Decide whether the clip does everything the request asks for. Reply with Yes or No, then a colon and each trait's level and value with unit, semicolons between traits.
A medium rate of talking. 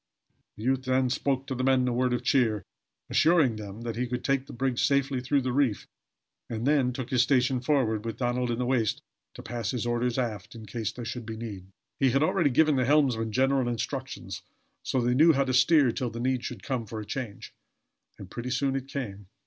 No: fast, 225 wpm